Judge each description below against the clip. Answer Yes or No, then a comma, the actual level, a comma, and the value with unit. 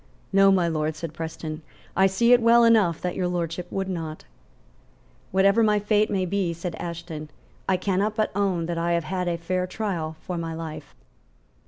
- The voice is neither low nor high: Yes, medium, 180 Hz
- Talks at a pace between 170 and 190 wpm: Yes, average, 185 wpm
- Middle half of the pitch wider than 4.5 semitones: No, average, 3.0 semitones